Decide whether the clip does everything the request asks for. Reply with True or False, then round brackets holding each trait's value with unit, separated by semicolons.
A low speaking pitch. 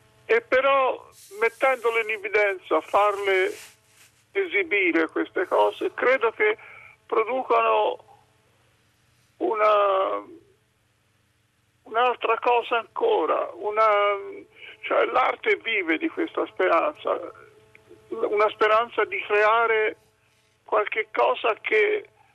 False (230 Hz)